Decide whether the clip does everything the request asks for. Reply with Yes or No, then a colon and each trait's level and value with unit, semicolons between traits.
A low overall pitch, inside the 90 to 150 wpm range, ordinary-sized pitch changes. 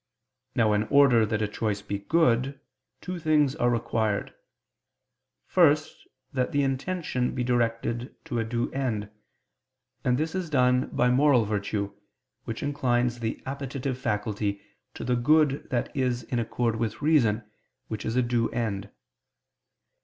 Yes: low, 120 Hz; average, 145 wpm; average, 3.5 semitones